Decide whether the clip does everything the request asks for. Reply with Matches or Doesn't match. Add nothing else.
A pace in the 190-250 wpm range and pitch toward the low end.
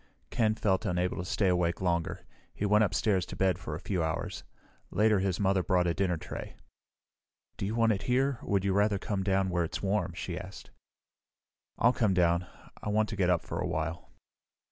Matches